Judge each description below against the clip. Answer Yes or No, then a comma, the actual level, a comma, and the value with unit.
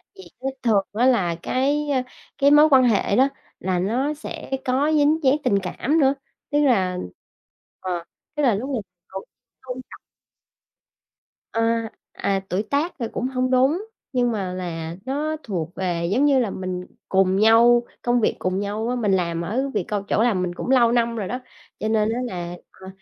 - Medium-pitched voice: No, high, 230 Hz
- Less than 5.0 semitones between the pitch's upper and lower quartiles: No, wide, 5.6 semitones